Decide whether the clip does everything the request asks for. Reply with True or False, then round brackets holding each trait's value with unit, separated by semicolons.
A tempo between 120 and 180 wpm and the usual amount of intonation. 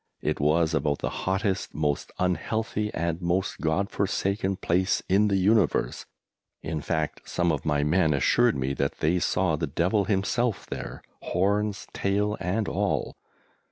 True (150 wpm; 4.0 semitones)